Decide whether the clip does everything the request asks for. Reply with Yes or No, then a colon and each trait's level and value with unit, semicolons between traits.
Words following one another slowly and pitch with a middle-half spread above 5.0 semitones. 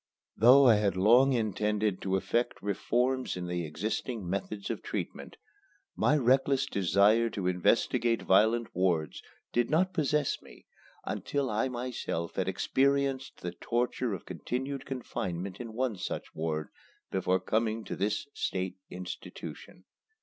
Yes: slow, 130 wpm; wide, 5.4 semitones